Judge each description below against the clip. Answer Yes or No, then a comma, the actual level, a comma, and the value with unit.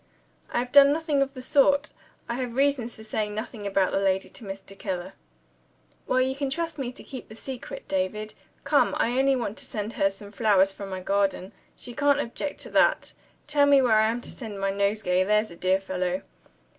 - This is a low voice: No, high, 220 Hz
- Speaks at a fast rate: Yes, fast, 210 wpm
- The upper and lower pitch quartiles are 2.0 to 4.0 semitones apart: No, average, 5.3 semitones